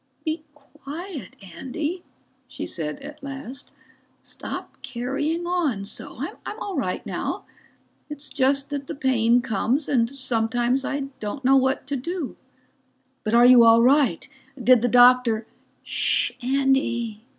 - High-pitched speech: Yes, very high, 265 Hz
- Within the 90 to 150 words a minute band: Yes, average, 140 wpm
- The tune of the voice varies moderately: Yes, average, 3.4 semitones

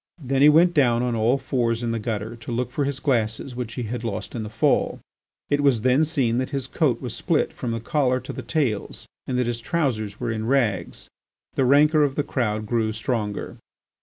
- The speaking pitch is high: No, low, 125 Hz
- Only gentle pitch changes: No, average, 3.3 semitones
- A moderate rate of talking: No, fast, 220 wpm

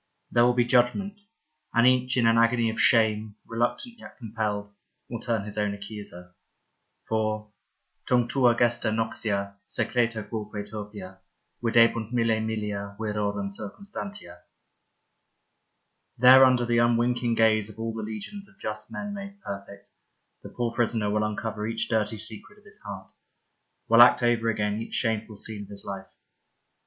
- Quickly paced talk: No, average, 150 wpm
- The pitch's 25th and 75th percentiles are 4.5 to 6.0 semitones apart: No, narrow, 2.4 semitones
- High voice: No, low, 110 Hz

